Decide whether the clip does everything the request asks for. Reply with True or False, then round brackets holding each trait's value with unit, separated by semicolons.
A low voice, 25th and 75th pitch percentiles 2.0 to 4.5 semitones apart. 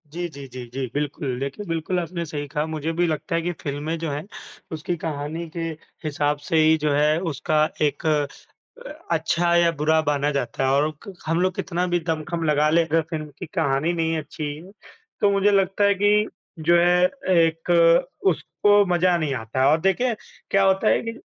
False (160 Hz; 2.9 semitones)